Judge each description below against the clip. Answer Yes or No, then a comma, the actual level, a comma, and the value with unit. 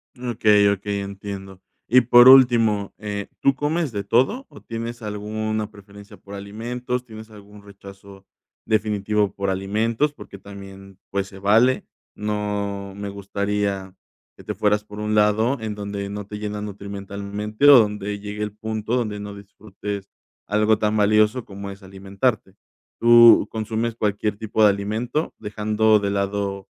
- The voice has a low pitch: Yes, low, 105 Hz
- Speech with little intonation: Yes, narrow, 1.6 semitones